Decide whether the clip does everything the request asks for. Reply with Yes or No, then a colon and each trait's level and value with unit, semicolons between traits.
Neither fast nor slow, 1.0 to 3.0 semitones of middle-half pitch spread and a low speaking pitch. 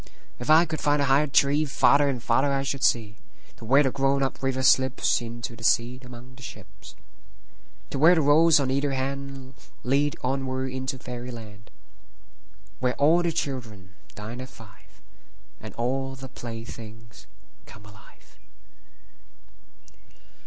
No: slow, 130 wpm; average, 2.7 semitones; low, 130 Hz